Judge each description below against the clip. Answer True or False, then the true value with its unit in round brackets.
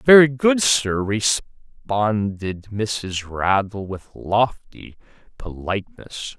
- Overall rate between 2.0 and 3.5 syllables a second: True (2.9 syllables/s)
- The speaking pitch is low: True (110 Hz)